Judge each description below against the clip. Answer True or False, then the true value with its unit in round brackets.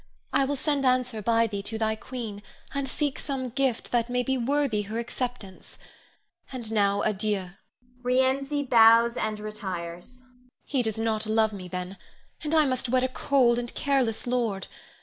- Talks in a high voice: True (235 Hz)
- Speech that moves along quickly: False (165 wpm)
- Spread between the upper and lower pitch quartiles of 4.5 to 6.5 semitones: False (3.4 semitones)